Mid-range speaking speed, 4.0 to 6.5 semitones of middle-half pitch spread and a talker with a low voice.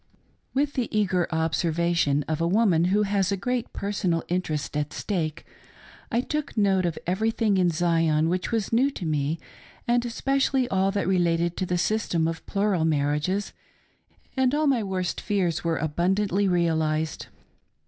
No: average, 155 wpm; average, 4.3 semitones; medium, 185 Hz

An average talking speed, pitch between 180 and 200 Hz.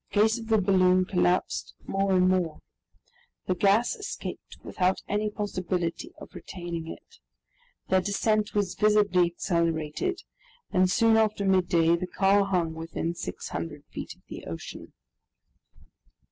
No: slow, 130 wpm; medium, 185 Hz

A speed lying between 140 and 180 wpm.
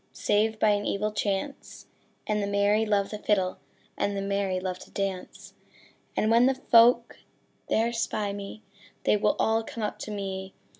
Yes: average, 170 wpm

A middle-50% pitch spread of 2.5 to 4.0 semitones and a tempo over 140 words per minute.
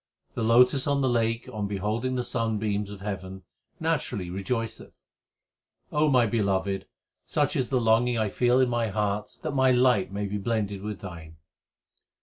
Yes: average, 3.7 semitones; average, 160 wpm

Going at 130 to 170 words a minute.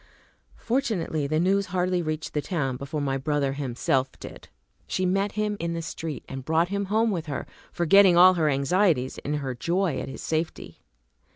No: average, 180 wpm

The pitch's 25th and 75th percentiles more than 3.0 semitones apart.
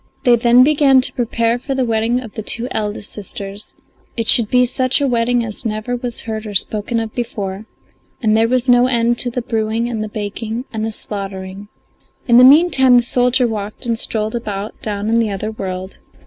No: narrow, 2.5 semitones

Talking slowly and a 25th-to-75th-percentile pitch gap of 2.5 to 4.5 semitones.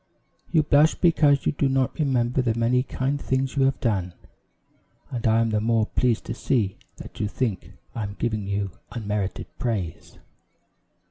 No: average, 165 wpm; average, 4.1 semitones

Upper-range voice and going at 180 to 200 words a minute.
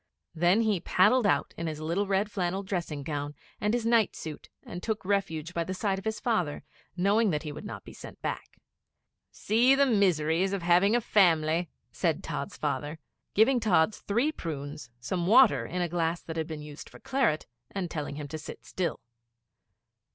No: medium, 180 Hz; average, 190 wpm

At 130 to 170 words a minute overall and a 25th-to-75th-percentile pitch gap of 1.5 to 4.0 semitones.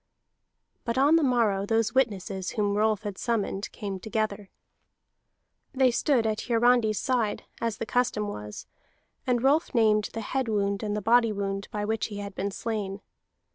Yes: average, 165 wpm; average, 2.8 semitones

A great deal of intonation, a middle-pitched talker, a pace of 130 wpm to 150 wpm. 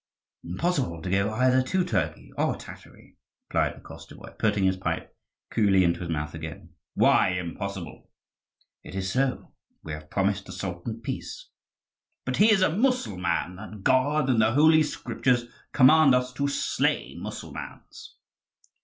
No: wide, 6.8 semitones; low, 110 Hz; average, 145 wpm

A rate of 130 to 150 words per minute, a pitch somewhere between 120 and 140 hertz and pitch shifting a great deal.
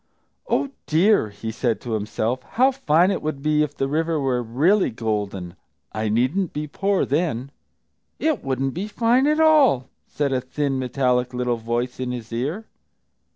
No: average, 165 wpm; low, 135 Hz; wide, 6.6 semitones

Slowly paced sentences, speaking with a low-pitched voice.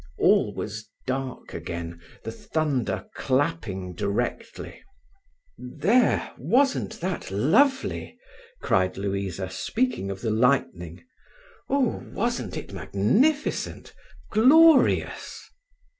Yes: slow, 85 wpm; low, 130 Hz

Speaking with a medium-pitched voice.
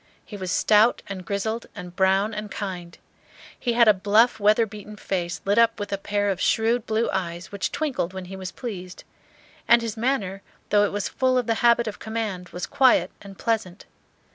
No: high, 205 Hz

